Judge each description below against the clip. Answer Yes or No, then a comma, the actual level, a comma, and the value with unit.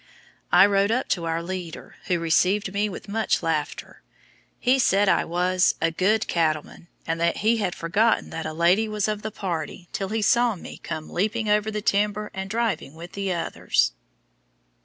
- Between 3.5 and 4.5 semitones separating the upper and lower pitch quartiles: Yes, average, 3.8 semitones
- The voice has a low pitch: No, high, 195 Hz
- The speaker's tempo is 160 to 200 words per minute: Yes, average, 180 wpm